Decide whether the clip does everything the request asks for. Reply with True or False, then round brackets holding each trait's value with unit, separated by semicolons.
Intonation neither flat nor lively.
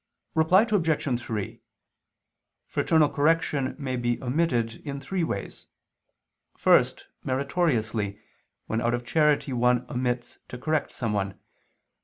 True (4.8 semitones)